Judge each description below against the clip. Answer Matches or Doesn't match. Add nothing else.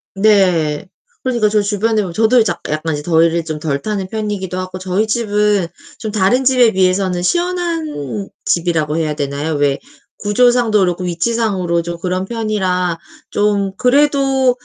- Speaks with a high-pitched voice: Matches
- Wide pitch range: Doesn't match